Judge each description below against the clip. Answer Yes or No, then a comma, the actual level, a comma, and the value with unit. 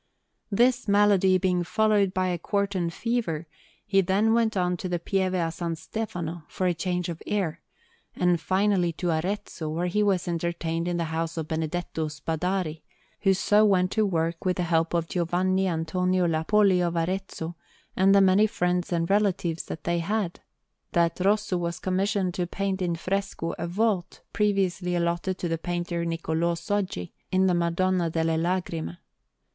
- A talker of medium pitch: Yes, medium, 180 Hz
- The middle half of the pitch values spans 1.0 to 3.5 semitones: Yes, narrow, 2.5 semitones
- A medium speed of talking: Yes, average, 165 wpm